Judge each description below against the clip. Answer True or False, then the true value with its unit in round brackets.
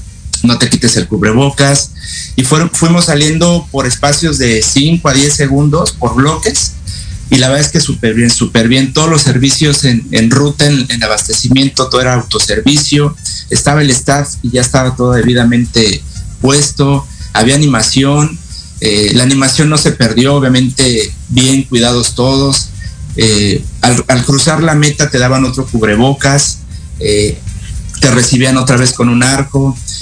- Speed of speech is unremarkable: True (155 wpm)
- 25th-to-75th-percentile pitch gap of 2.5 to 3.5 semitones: False (4.2 semitones)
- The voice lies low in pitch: True (130 Hz)